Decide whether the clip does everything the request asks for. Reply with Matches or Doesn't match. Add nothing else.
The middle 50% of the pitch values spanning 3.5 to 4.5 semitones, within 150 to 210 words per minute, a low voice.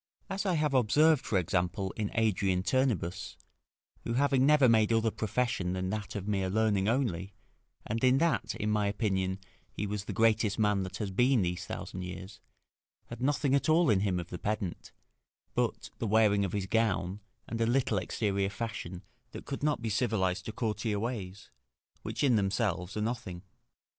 Matches